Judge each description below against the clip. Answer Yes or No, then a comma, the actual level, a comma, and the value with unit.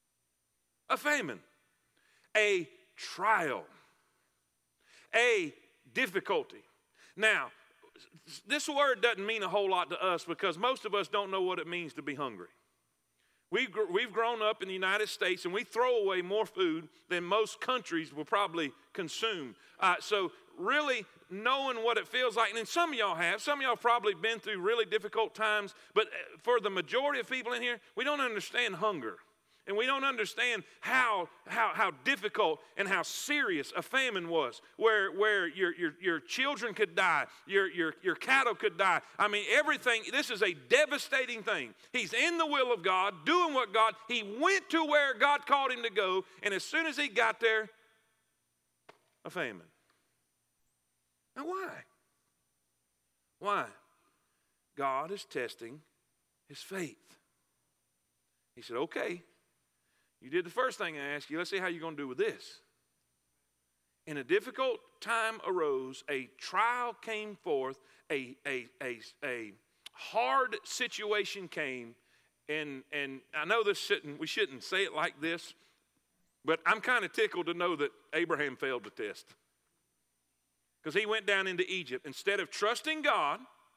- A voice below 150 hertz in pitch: No, high, 210 Hz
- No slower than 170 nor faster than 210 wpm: No, average, 160 wpm